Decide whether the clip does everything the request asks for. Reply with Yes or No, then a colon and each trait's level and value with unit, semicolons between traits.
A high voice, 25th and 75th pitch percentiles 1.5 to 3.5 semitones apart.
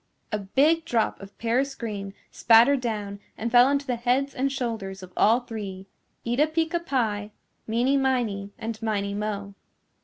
No: high, 230 Hz; average, 4.5 semitones